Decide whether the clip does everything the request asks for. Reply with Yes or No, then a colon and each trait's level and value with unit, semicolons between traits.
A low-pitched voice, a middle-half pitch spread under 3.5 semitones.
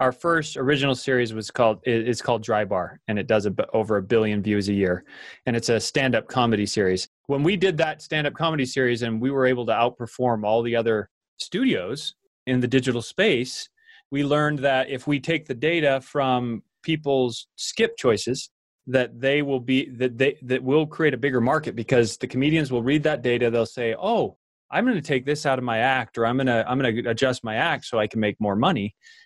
No: low, 130 Hz; average, 3.8 semitones